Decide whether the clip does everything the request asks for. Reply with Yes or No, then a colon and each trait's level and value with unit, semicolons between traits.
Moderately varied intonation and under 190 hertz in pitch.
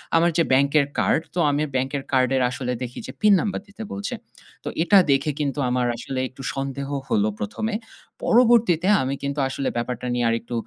Yes: average, 3.7 semitones; low, 135 Hz